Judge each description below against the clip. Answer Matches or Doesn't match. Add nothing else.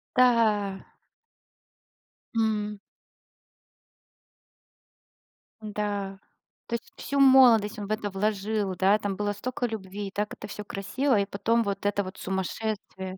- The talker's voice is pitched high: Matches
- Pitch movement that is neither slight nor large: Doesn't match